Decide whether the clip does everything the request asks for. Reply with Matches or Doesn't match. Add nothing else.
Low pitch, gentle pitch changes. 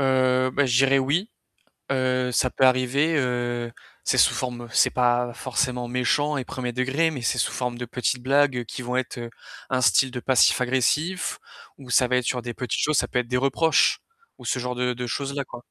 Matches